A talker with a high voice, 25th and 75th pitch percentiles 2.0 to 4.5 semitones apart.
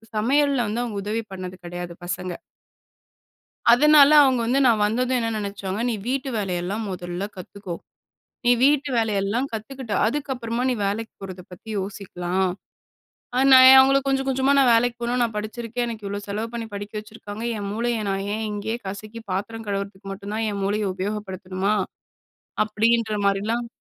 Yes: high, 215 Hz; average, 3.3 semitones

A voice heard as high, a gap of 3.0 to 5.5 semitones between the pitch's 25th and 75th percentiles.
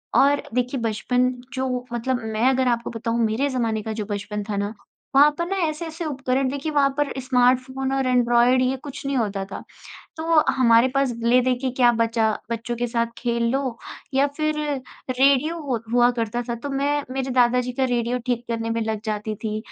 No: very high, 250 Hz; narrow, 2.6 semitones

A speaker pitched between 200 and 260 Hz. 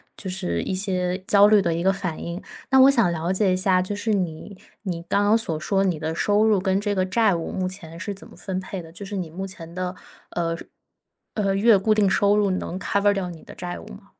No: high, 190 Hz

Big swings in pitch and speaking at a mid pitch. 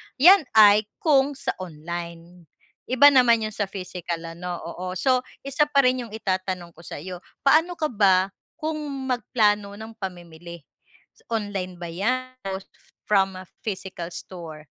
No: wide, 6.1 semitones; high, 195 Hz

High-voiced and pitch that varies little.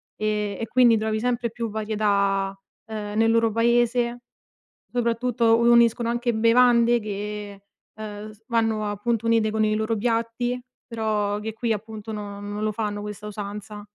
Yes: high, 220 Hz; narrow, 1.9 semitones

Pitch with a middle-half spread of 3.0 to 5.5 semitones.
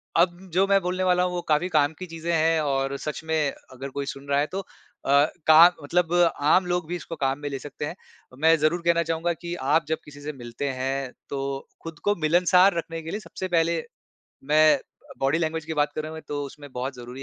Yes: average, 3.3 semitones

